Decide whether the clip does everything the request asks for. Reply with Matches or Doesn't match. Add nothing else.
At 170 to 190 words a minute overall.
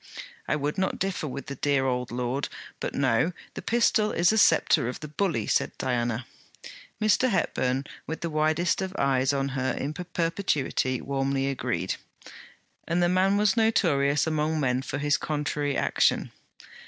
Doesn't match